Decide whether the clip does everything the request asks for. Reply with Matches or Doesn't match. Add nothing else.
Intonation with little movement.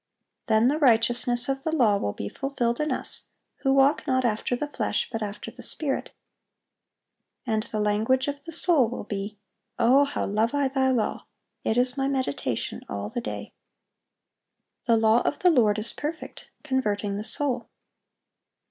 Doesn't match